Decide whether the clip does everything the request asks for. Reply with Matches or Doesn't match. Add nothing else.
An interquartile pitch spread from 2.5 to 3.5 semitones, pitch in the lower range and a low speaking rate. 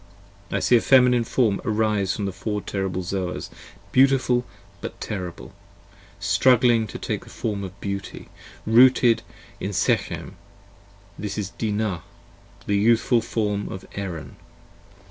Matches